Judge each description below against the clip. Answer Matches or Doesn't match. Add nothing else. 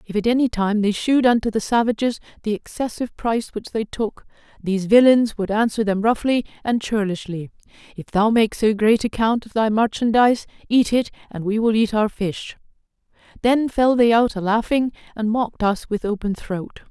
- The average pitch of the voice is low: Doesn't match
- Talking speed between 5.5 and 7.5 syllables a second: Matches